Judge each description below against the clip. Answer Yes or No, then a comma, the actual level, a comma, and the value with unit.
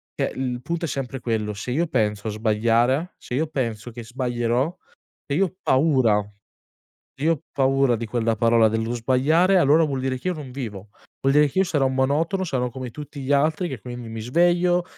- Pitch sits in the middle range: No, low, 130 Hz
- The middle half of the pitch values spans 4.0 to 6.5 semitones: Yes, average, 4.5 semitones